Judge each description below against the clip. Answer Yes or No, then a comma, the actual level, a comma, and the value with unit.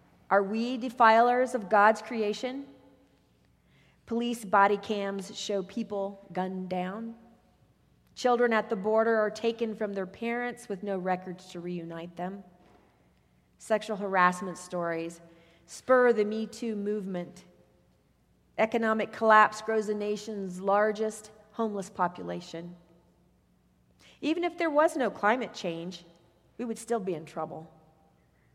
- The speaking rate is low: Yes, slow, 120 wpm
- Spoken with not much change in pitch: No, average, 4.0 semitones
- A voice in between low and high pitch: No, high, 210 Hz